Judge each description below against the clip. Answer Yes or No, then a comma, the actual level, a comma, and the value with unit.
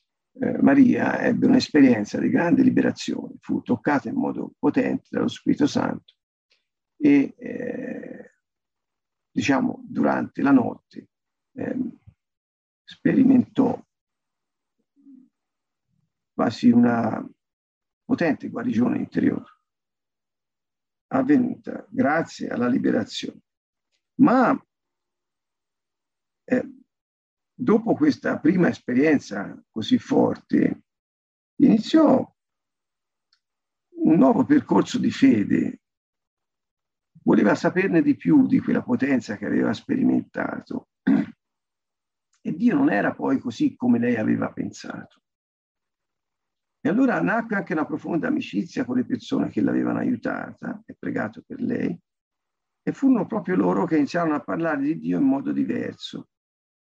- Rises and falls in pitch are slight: Yes, narrow, 1.6 semitones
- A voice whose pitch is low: No, very high, 255 Hz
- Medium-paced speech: No, slow, 100 wpm